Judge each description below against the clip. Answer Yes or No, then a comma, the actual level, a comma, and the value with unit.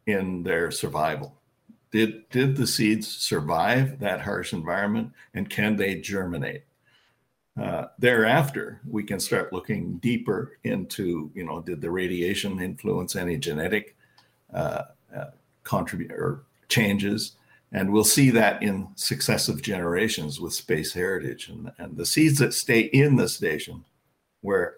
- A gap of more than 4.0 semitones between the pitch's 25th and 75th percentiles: Yes, average, 4.6 semitones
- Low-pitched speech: Yes, low, 110 Hz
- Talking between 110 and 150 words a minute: Yes, slow, 135 wpm